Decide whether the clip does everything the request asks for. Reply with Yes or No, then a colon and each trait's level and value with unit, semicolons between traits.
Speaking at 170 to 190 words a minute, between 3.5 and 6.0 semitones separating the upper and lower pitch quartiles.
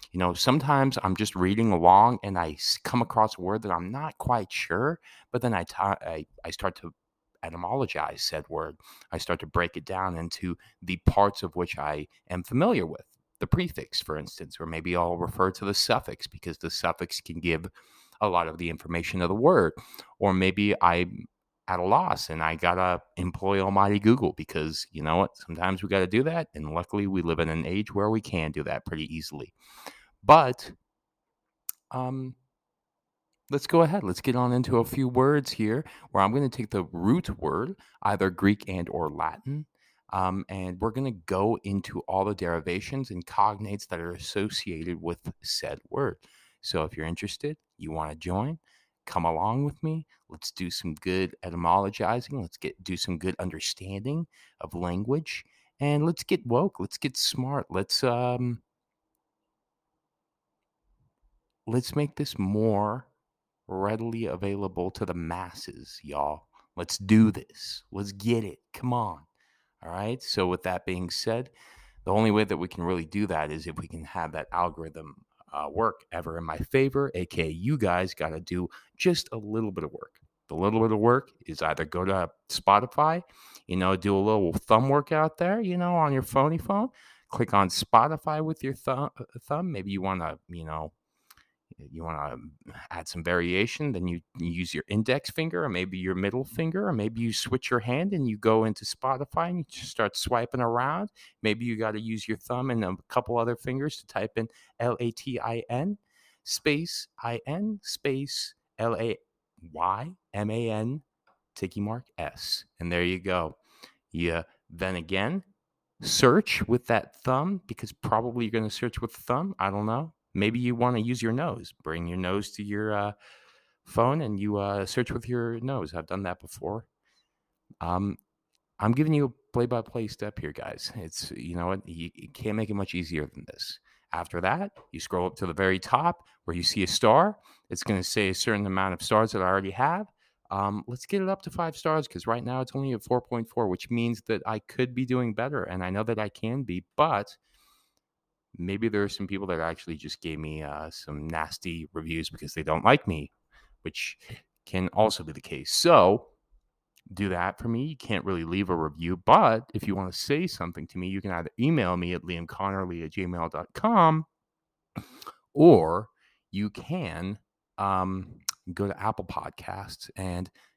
Yes: average, 185 wpm; wide, 5.6 semitones